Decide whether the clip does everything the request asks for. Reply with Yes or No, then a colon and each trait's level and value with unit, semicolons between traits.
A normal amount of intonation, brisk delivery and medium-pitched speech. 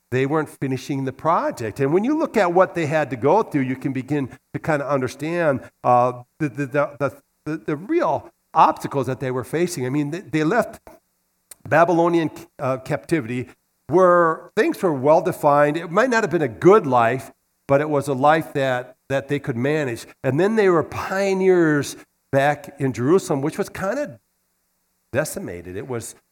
No: average, 3.9 semitones; average, 185 wpm; medium, 150 Hz